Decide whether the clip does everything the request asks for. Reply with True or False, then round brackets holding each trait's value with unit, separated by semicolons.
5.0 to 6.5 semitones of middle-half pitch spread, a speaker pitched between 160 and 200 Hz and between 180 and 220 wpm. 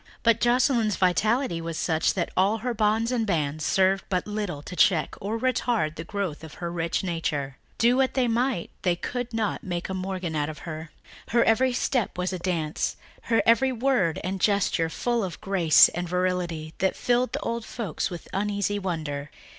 True (5.5 semitones; 190 Hz; 185 wpm)